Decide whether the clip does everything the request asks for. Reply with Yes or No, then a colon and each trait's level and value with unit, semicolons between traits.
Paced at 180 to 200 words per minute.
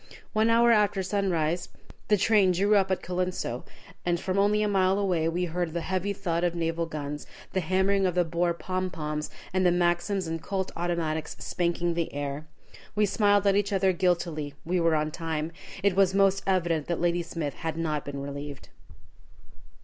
Yes: average, 185 wpm